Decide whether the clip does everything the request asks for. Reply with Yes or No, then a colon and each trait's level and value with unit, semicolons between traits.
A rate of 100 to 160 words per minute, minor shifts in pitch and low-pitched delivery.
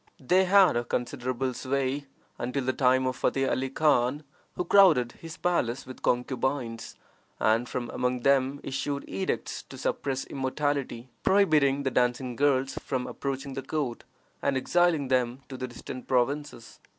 Yes: average, 145 wpm; narrow, 2.3 semitones; low, 130 Hz